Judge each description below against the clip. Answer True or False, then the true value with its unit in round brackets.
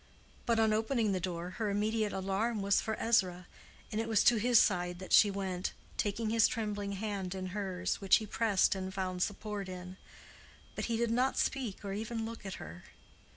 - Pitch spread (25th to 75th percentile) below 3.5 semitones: True (2.9 semitones)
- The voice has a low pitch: False (205 Hz)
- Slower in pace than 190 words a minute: False (195 wpm)